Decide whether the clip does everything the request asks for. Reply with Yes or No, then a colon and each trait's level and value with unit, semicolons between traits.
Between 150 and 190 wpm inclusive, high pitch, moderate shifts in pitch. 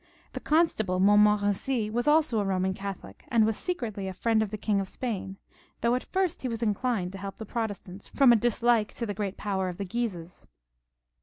No: fast, 205 wpm; high, 210 Hz; average, 3.5 semitones